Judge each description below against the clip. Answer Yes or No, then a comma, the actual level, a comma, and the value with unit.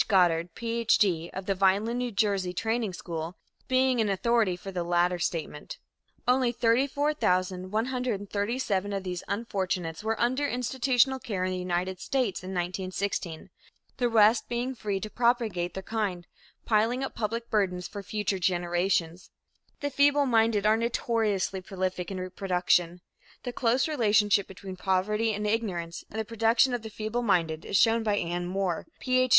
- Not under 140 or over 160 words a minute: Yes, average, 145 wpm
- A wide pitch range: No, average, 4.2 semitones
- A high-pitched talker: Yes, high, 205 Hz